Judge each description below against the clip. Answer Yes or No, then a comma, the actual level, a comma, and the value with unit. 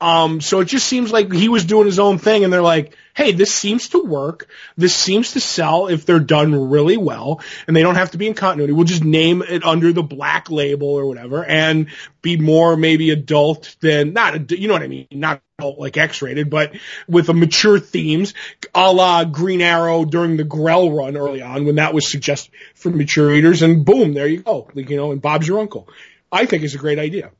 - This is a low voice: No, medium, 165 Hz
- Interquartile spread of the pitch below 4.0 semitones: Yes, average, 3.5 semitones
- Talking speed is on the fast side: Yes, fast, 230 wpm